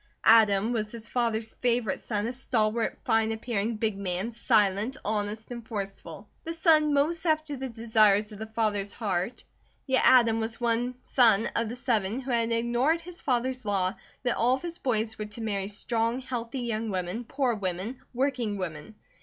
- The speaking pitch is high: Yes, high, 230 Hz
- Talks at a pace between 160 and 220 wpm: Yes, average, 180 wpm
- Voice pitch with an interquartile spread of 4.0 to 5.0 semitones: No, average, 2.9 semitones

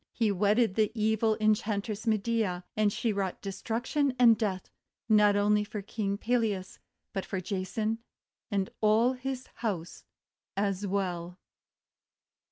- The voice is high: Yes, high, 210 Hz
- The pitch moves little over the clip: Yes, narrow, 2.3 semitones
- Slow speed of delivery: Yes, slow, 130 wpm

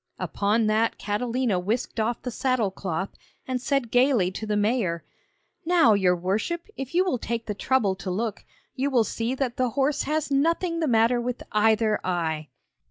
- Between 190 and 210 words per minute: No, average, 175 wpm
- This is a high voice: Yes, high, 230 Hz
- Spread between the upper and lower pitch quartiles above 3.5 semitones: Yes, average, 4.2 semitones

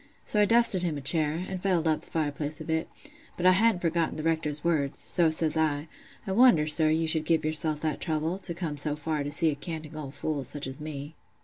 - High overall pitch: No, medium, 160 Hz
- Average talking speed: No, fast, 235 wpm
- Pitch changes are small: Yes, narrow, 2.1 semitones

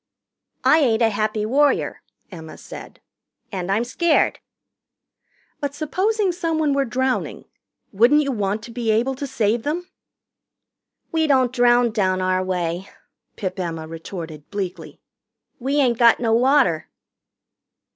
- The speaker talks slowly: Yes, slow, 130 wpm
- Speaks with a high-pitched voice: Yes, high, 235 Hz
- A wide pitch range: Yes, wide, 6.5 semitones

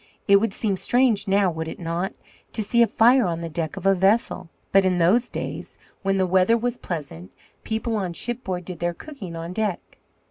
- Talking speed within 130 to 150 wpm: No, fast, 205 wpm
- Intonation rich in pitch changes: No, average, 4.3 semitones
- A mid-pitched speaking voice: No, high, 195 Hz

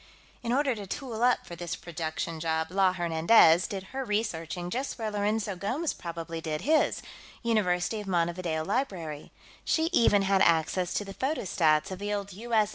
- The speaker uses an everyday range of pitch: Yes, average, 4.9 semitones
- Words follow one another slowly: No, average, 170 wpm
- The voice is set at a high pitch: Yes, high, 195 Hz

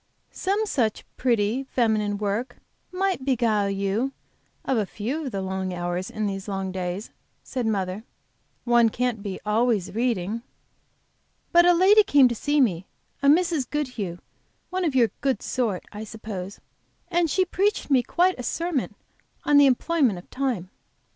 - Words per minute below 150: No, average, 155 wpm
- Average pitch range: No, wide, 6.1 semitones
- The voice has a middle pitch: No, high, 235 Hz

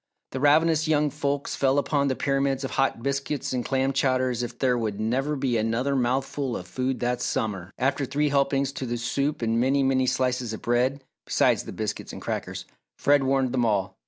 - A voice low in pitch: Yes, low, 130 Hz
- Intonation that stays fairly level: Yes, narrow, 2.3 semitones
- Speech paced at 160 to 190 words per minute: No, average, 200 wpm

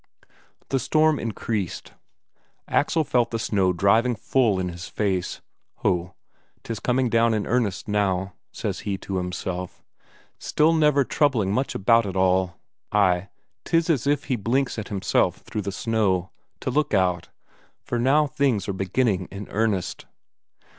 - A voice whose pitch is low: Yes, low, 105 Hz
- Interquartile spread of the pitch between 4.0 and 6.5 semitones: Yes, average, 5.2 semitones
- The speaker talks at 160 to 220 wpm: No, average, 145 wpm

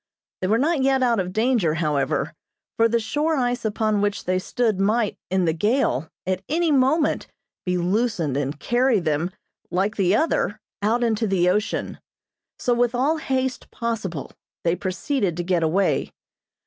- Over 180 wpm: No, average, 160 wpm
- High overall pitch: Yes, high, 215 Hz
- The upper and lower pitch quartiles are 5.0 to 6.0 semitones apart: Yes, wide, 5.4 semitones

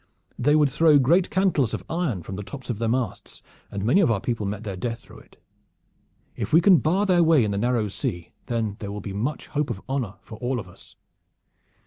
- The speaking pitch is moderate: No, low, 120 Hz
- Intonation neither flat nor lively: No, wide, 6.7 semitones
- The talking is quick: Yes, fast, 225 wpm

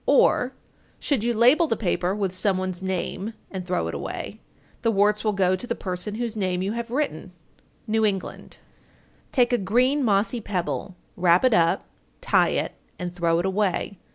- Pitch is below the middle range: No, high, 200 Hz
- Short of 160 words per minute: No, average, 180 wpm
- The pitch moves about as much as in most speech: Yes, average, 3.7 semitones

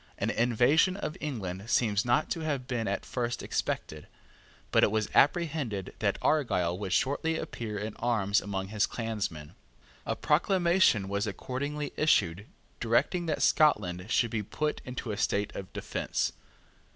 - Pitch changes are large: Yes, wide, 6.7 semitones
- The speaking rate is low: No, average, 150 wpm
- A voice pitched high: No, low, 115 Hz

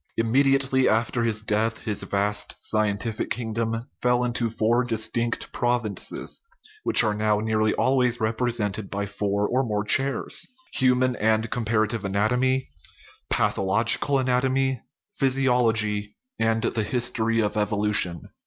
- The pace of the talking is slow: Yes, slow, 125 wpm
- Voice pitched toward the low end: Yes, low, 115 Hz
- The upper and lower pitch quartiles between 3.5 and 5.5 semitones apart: No, average, 2.7 semitones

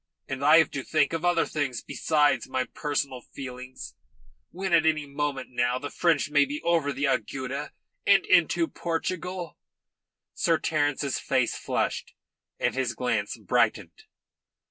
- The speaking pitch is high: No, medium, 145 Hz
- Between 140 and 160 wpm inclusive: Yes, average, 145 wpm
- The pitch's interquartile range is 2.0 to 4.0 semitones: Yes, average, 3.6 semitones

